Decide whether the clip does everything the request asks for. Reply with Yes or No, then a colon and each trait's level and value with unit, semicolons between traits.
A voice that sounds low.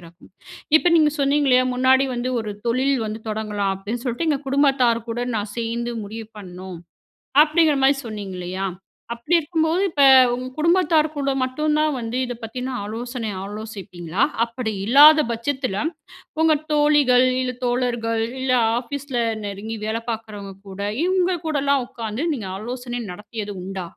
No: high, 245 Hz